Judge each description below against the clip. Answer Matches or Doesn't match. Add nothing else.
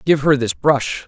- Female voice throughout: Doesn't match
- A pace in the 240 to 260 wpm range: Doesn't match